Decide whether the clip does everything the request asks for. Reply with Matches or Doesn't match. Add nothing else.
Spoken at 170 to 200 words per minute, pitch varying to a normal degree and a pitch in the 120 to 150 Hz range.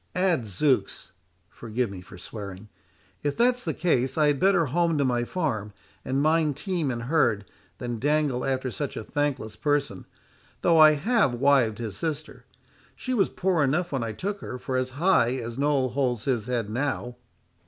Matches